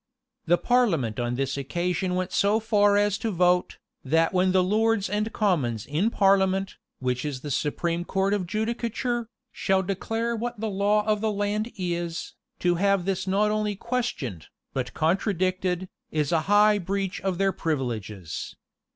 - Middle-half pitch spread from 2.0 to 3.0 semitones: No, average, 4.0 semitones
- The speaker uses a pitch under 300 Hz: Yes, high, 190 Hz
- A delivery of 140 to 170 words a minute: Yes, average, 160 wpm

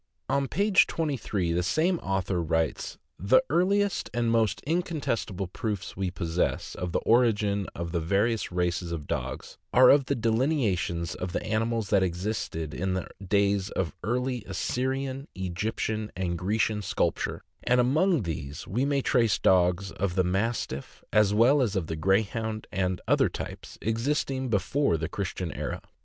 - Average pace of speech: Yes, average, 150 wpm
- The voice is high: No, low, 105 Hz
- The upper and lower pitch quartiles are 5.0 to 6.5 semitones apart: Yes, wide, 5.5 semitones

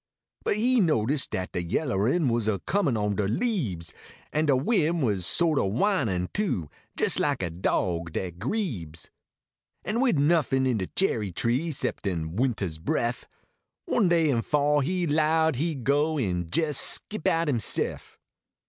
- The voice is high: No, low, 135 Hz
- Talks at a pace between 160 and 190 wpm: Yes, average, 165 wpm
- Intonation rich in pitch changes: Yes, wide, 8.8 semitones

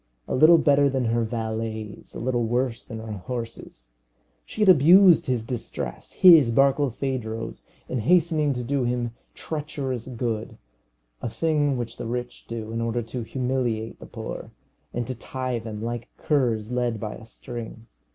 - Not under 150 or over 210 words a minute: Yes, average, 160 wpm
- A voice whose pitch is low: Yes, low, 120 Hz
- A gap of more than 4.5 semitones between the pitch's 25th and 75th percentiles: No, average, 3.1 semitones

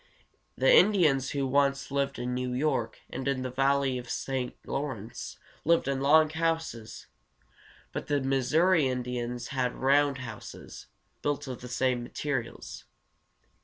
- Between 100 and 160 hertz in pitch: Yes, low, 135 Hz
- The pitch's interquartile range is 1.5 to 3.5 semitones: Yes, narrow, 2.5 semitones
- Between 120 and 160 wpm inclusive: Yes, average, 145 wpm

